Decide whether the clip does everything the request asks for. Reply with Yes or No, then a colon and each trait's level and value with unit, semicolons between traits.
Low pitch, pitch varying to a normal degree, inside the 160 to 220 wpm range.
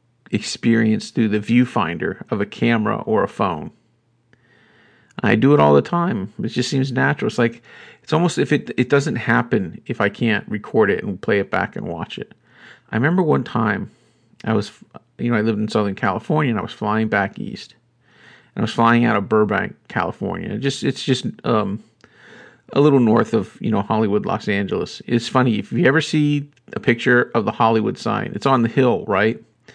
Yes: low, 120 Hz; average, 3.3 semitones; average, 200 wpm